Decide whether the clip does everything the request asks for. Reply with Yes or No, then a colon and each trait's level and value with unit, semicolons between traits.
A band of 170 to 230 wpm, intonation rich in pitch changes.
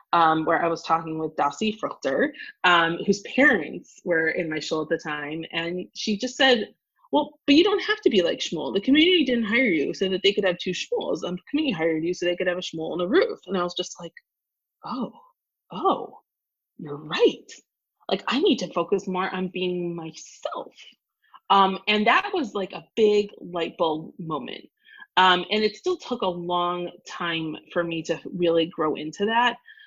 Yes: average, 200 wpm; wide, 8.3 semitones